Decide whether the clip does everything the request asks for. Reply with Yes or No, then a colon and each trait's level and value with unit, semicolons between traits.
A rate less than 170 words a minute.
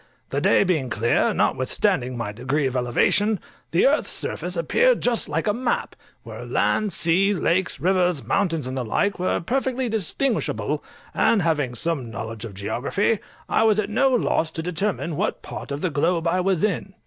No: average, 175 wpm